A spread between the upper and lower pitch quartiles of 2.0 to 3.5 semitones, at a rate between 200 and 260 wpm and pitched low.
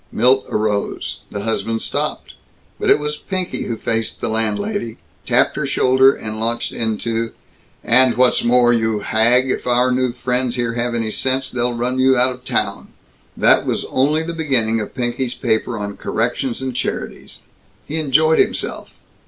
No: narrow, 2.6 semitones; average, 165 wpm; low, 120 Hz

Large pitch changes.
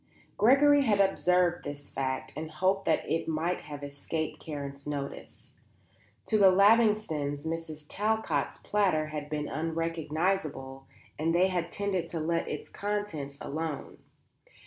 No: average, 4.7 semitones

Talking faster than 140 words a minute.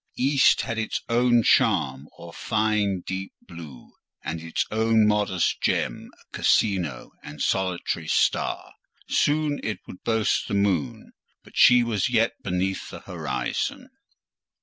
No: slow, 135 wpm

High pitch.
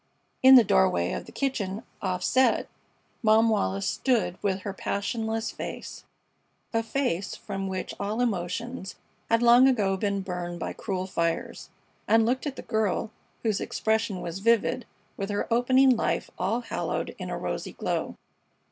Yes: high, 215 Hz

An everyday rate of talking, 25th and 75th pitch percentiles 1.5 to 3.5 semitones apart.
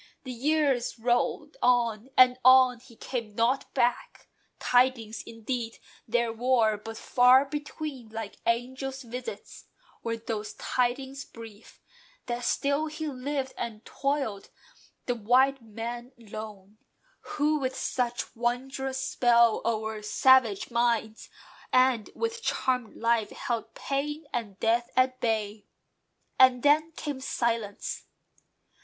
No: slow, 115 wpm; narrow, 2.6 semitones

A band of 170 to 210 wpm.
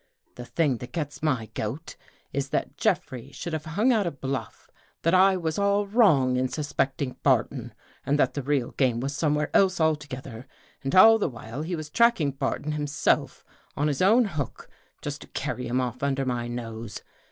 Yes: average, 185 wpm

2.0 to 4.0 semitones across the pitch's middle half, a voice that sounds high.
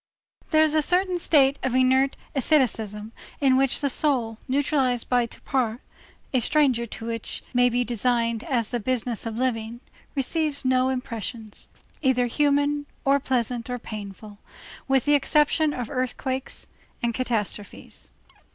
Yes: average, 3.3 semitones; very high, 255 Hz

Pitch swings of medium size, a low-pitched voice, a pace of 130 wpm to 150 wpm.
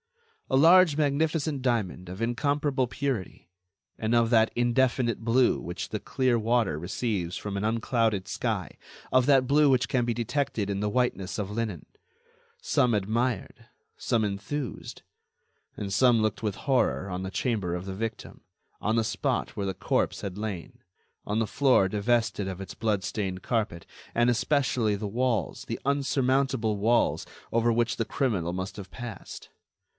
No: average, 4.2 semitones; low, 115 Hz; average, 160 wpm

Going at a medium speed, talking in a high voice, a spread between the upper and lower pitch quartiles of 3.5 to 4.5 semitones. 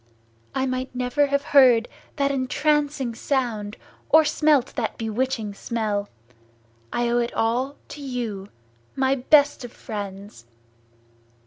No: slow, 120 wpm; very high, 250 Hz; average, 3.8 semitones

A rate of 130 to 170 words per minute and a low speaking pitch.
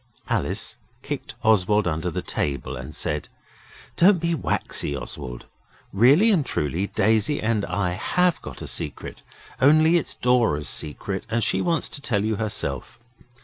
Yes: average, 145 wpm; low, 110 Hz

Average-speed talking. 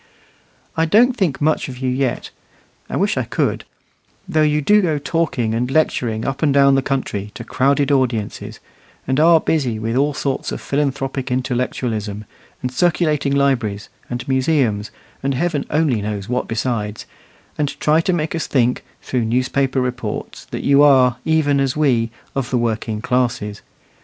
Yes: average, 160 wpm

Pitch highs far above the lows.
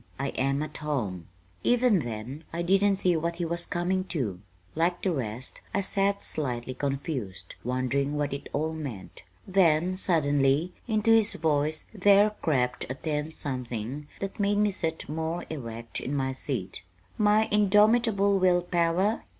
Yes: wide, 6.0 semitones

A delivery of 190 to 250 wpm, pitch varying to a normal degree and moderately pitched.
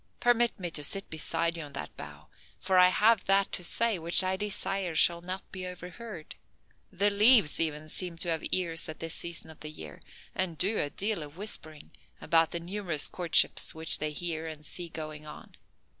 Yes: average, 195 wpm; average, 3.5 semitones; medium, 170 Hz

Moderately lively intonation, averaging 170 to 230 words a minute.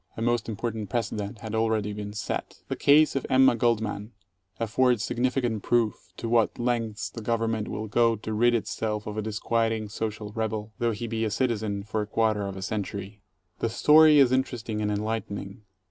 No: narrow, 2.0 semitones; average, 185 wpm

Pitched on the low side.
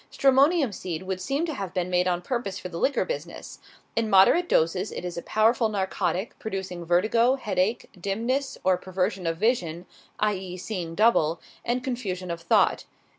No: high, 190 Hz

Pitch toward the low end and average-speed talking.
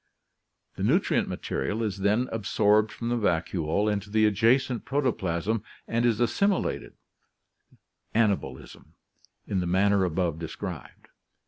No: low, 105 Hz; slow, 115 wpm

